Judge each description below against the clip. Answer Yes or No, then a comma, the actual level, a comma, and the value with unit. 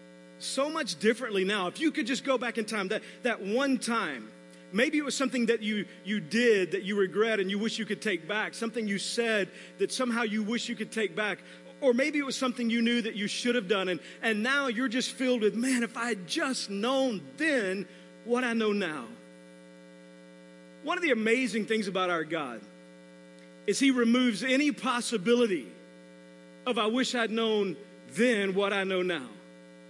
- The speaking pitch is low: No, high, 220 Hz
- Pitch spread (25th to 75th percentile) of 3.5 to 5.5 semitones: Yes, average, 5.1 semitones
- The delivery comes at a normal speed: Yes, average, 195 wpm